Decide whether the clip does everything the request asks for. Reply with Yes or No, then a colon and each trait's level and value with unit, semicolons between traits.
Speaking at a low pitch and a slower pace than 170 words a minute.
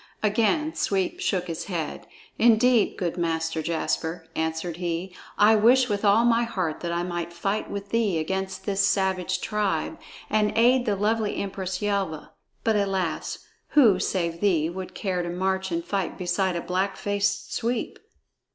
No: high, 190 Hz; average, 160 wpm